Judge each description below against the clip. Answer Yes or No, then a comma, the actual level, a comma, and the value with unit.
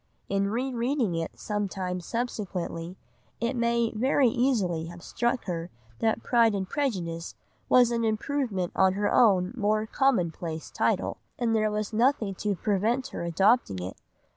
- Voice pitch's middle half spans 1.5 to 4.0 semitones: No, average, 4.7 semitones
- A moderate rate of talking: Yes, average, 155 wpm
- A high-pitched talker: Yes, high, 215 Hz